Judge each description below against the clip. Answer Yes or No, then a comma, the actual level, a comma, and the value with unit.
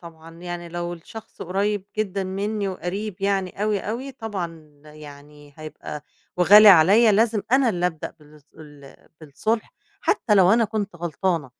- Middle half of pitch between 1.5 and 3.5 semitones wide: No, average, 4.7 semitones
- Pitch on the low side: No, medium, 185 Hz